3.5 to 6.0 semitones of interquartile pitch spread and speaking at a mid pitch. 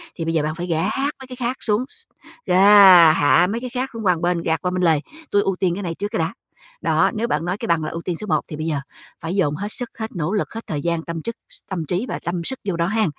Yes: average, 4.2 semitones; medium, 180 Hz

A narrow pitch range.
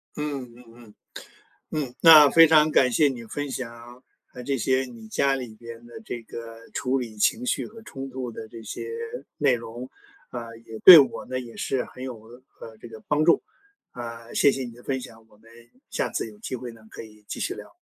No: average, 3.1 semitones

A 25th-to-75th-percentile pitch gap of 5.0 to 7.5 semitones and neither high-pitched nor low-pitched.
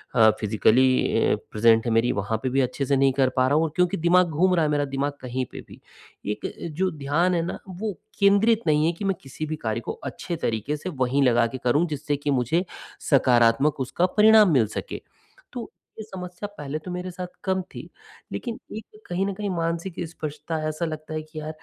Yes: wide, 5.5 semitones; medium, 155 Hz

